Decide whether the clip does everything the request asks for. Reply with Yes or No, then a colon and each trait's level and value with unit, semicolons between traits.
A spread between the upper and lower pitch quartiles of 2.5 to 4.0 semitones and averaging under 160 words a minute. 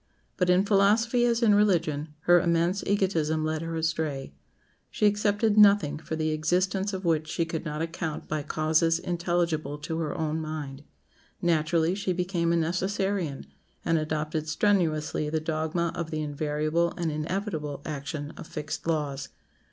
Yes: average, 2.9 semitones; average, 150 wpm